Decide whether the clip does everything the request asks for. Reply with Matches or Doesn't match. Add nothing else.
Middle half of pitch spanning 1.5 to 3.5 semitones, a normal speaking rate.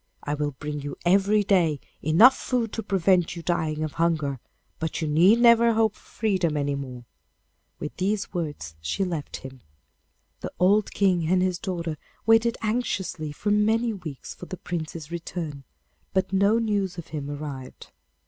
Doesn't match